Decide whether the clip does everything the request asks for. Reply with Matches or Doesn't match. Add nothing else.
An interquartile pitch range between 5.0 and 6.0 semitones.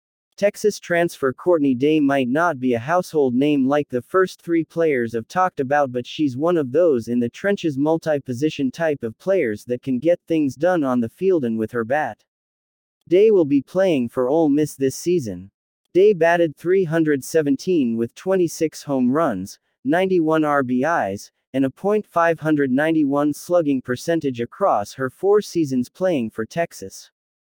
Matches